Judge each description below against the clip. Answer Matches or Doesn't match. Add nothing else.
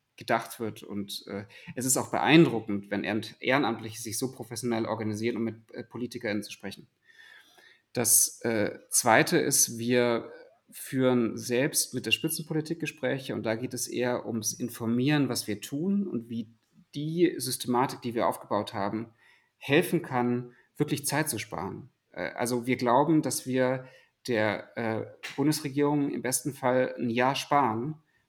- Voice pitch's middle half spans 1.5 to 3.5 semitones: Doesn't match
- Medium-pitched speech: Doesn't match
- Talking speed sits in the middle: Matches